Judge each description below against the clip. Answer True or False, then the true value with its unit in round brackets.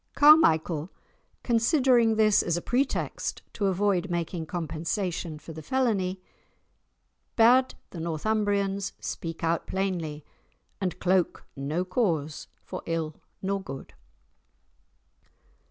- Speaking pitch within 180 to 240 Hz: True (185 Hz)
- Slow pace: True (105 wpm)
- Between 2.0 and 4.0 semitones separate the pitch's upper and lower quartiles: False (4.6 semitones)